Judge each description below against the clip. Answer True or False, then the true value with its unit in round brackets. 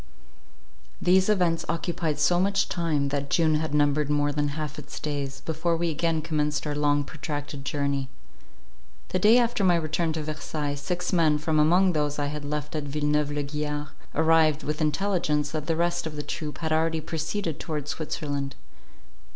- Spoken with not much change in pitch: True (2.0 semitones)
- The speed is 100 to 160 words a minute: False (175 wpm)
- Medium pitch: True (150 Hz)